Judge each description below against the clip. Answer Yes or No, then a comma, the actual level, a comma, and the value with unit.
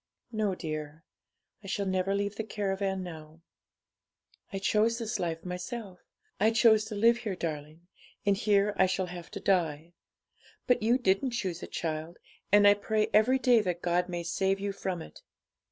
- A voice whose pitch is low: No, high, 195 Hz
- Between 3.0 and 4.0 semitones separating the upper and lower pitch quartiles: Yes, average, 3.5 semitones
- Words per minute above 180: No, average, 170 wpm